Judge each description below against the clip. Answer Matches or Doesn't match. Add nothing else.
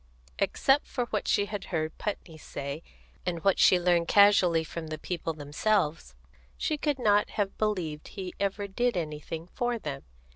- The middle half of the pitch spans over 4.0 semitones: Matches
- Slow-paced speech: Doesn't match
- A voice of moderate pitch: Matches